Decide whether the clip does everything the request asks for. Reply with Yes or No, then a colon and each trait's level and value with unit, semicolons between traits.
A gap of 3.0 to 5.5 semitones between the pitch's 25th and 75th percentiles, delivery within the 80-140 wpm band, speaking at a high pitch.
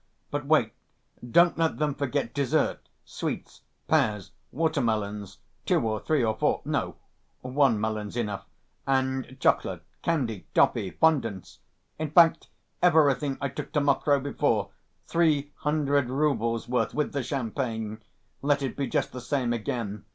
No: average, 4.7 semitones; slow, 135 wpm; low, 135 Hz